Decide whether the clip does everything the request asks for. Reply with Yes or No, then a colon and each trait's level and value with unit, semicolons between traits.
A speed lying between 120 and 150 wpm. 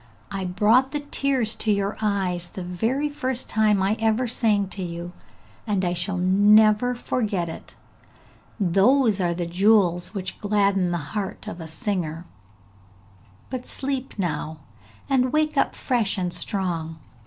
Yes: average, 145 wpm